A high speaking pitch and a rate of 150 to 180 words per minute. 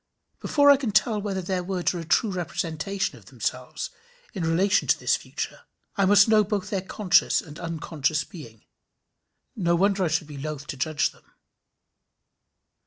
No: medium, 180 Hz; average, 170 wpm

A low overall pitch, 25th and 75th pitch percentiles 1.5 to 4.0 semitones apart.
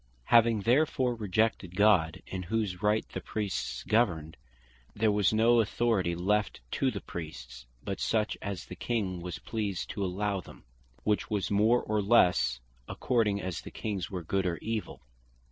Yes: low, 105 Hz; average, 3.3 semitones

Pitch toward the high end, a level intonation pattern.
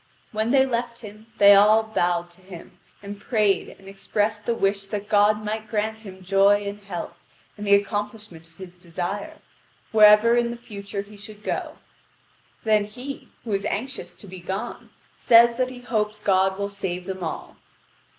Yes: high, 205 Hz; narrow, 2.0 semitones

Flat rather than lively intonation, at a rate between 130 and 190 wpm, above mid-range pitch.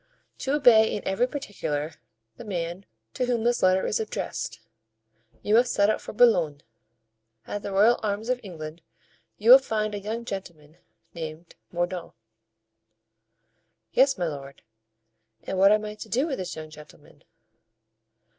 No: average, 5.1 semitones; average, 150 wpm; high, 200 Hz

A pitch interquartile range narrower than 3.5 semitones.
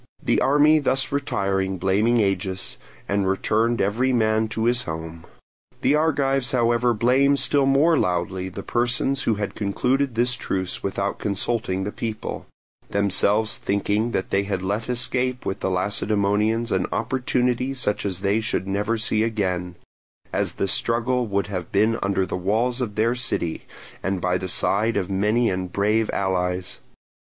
No: average, 4.0 semitones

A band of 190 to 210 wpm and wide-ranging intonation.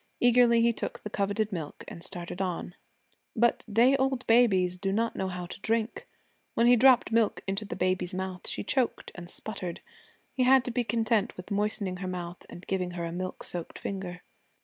No: average, 195 wpm; average, 4.2 semitones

